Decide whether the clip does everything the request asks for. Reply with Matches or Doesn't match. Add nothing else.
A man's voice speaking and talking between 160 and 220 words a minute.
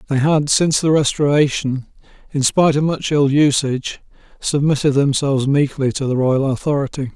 Doesn't match